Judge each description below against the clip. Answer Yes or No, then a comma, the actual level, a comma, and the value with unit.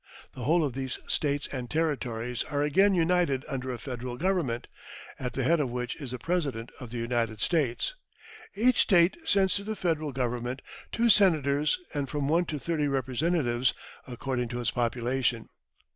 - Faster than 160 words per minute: Yes, average, 170 wpm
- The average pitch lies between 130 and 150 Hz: Yes, low, 135 Hz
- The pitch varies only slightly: No, average, 5.1 semitones